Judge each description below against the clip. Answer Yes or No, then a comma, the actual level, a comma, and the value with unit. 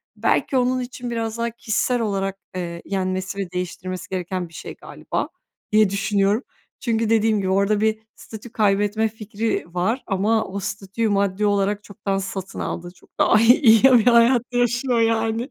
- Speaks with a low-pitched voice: No, high, 215 Hz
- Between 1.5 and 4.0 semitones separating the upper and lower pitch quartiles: Yes, average, 2.7 semitones